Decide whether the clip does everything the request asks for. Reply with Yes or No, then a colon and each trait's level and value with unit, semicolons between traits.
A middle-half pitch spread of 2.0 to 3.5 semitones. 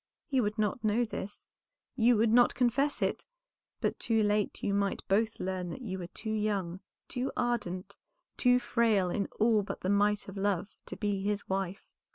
Yes: average, 3.0 semitones